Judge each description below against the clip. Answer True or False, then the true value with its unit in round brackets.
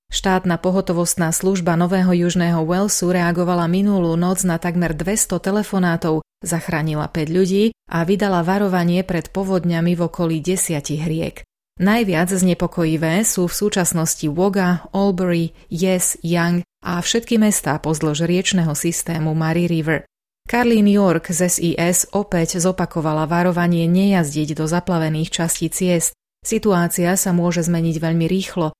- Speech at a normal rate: True (125 wpm)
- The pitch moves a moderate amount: False (2.1 semitones)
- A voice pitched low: False (175 Hz)